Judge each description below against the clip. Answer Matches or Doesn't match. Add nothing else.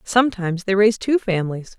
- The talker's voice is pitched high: Matches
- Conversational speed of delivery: Matches